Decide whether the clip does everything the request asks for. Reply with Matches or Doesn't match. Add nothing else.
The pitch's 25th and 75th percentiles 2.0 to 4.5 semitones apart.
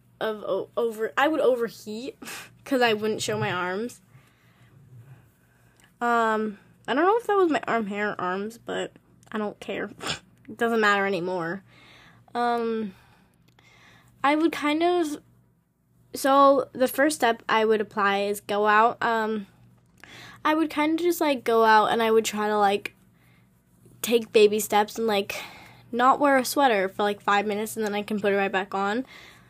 Matches